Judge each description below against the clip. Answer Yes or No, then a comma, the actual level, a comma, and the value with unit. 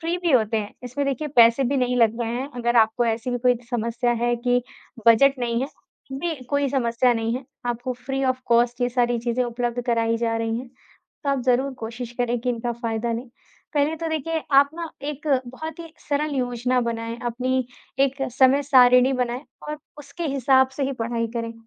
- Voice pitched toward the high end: Yes, high, 245 Hz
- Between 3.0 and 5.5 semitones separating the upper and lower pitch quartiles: No, narrow, 2.5 semitones